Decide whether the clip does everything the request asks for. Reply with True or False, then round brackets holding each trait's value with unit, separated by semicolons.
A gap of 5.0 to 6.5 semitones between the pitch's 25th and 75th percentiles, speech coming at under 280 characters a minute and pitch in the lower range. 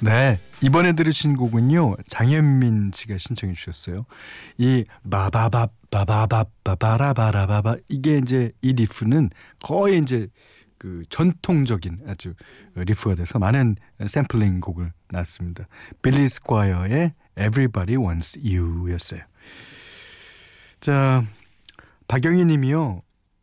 True (5.5 semitones; 265 characters per minute; 110 Hz)